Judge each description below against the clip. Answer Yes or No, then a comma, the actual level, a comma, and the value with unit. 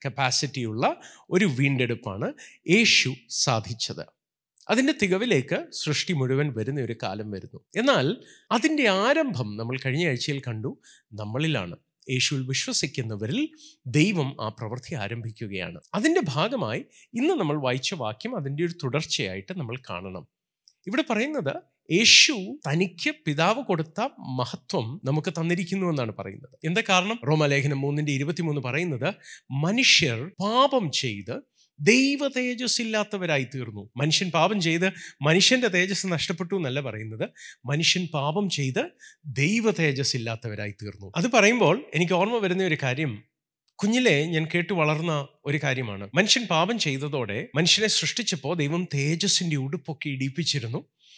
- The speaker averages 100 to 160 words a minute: Yes, average, 115 wpm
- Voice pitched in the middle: Yes, medium, 155 Hz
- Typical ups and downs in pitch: No, wide, 6.2 semitones